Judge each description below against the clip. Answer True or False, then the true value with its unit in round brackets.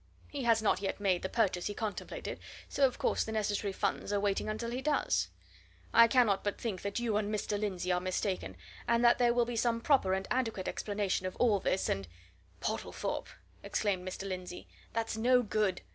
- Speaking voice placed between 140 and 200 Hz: False (210 Hz)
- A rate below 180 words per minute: False (200 wpm)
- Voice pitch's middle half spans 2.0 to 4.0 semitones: True (3.6 semitones)